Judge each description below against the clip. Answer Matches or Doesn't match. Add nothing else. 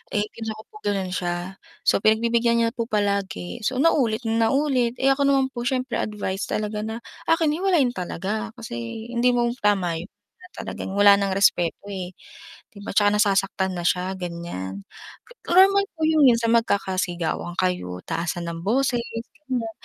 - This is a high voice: Matches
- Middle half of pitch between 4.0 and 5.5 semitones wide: Matches